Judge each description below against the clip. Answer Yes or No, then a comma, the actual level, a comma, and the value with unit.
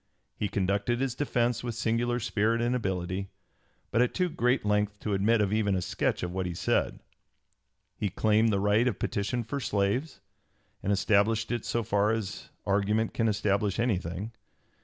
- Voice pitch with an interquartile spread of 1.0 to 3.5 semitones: Yes, average, 2.9 semitones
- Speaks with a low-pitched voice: Yes, low, 105 Hz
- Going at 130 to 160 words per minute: No, average, 170 wpm